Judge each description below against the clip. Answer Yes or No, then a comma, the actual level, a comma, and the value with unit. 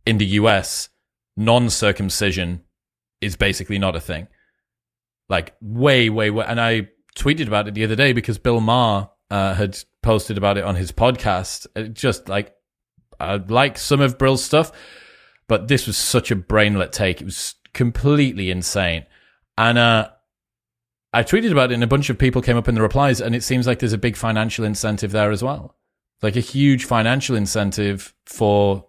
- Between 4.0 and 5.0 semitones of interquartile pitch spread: No, average, 3.3 semitones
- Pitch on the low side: Yes, low, 110 Hz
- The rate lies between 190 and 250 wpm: No, average, 180 wpm